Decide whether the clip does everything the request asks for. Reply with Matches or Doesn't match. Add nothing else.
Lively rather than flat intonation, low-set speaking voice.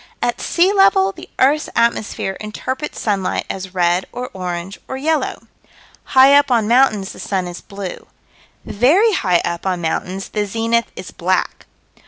Doesn't match